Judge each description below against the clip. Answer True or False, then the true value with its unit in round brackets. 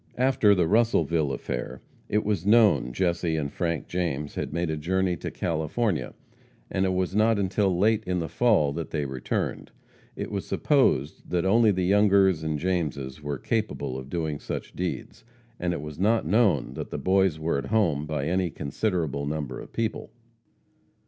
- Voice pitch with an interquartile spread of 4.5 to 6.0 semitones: True (5.0 semitones)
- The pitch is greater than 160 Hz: False (90 Hz)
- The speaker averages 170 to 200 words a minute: True (175 wpm)